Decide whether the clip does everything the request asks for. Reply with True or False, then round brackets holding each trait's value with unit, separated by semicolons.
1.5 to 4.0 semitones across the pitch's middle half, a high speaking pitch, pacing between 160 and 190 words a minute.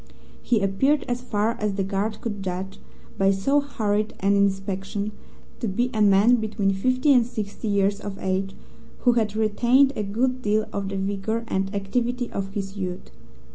True (3.2 semitones; 205 Hz; 175 wpm)